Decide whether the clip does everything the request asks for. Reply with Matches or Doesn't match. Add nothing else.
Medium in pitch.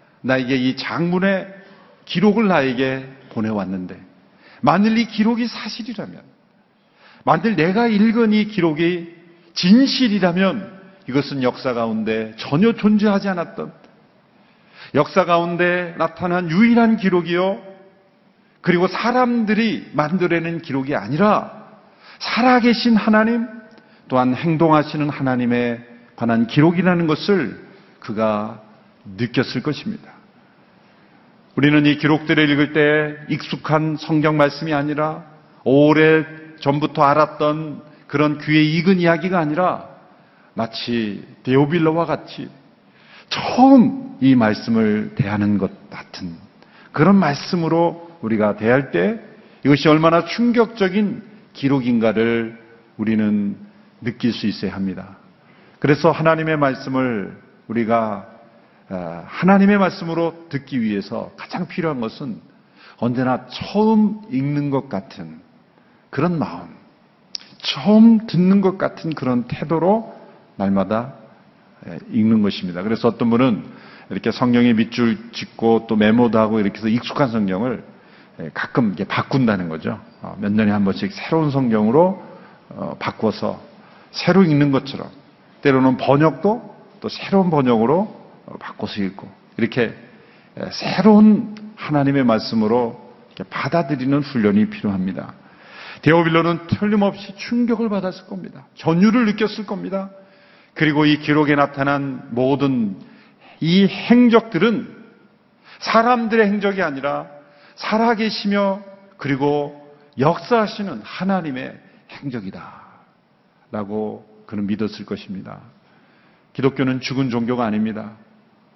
Matches